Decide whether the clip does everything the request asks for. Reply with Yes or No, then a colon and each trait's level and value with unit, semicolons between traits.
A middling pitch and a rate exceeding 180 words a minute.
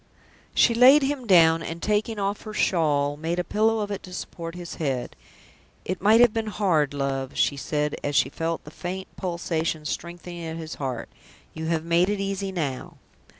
Yes: medium, 170 Hz; average, 190 wpm